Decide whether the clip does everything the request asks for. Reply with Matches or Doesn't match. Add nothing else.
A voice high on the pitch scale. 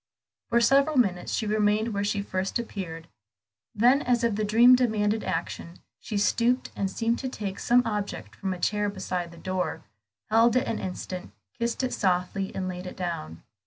Matches